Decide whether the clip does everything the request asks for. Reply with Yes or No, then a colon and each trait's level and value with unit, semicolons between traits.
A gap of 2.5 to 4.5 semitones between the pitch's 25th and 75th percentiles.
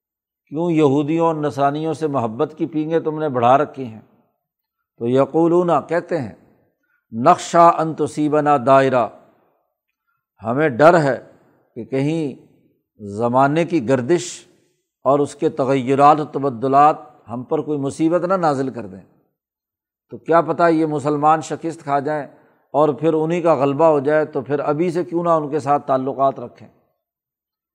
Yes: average, 3.1 semitones